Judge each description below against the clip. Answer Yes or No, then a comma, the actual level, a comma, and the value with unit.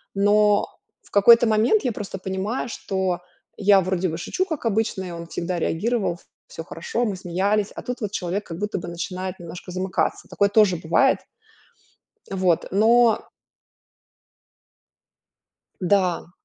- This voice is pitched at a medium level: No, high, 195 Hz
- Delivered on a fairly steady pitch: No, average, 3.1 semitones